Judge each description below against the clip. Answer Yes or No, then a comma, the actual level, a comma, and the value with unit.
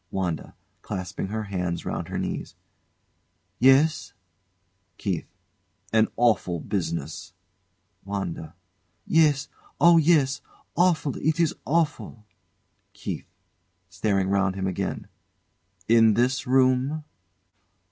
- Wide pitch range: Yes, wide, 7.4 semitones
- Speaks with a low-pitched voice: Yes, low, 115 Hz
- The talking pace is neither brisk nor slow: No, slow, 95 wpm